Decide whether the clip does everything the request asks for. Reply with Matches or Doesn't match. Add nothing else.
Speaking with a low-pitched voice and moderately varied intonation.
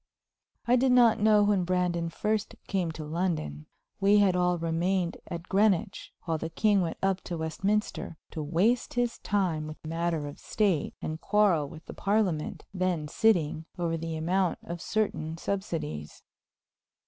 Doesn't match